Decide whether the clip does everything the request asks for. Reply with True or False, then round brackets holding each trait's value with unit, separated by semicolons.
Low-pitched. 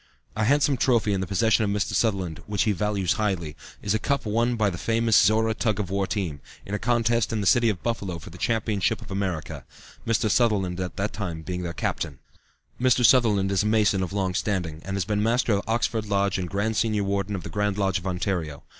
True (100 Hz)